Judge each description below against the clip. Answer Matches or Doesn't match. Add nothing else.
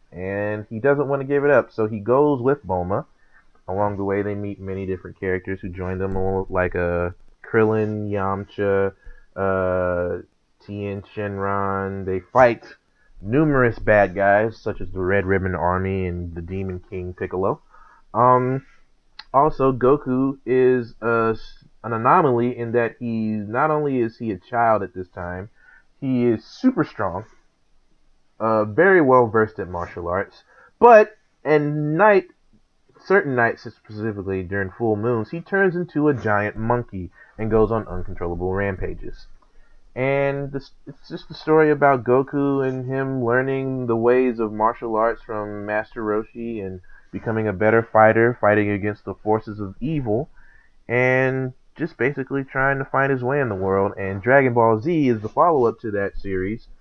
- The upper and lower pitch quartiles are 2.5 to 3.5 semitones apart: Doesn't match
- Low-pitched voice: Matches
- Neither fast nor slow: Matches